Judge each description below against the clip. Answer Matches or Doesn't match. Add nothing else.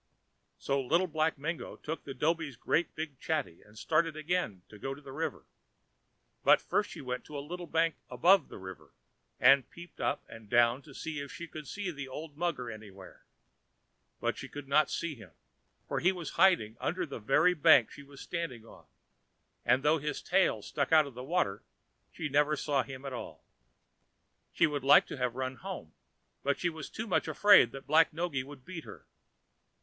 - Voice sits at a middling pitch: Matches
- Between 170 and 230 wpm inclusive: Matches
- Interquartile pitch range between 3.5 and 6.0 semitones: Matches